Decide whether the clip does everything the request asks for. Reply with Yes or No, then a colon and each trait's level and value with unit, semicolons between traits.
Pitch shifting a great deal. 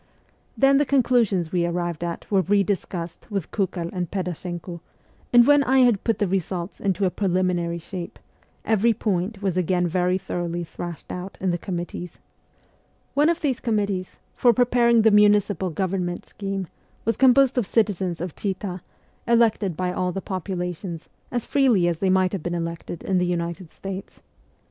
No: average, 3.3 semitones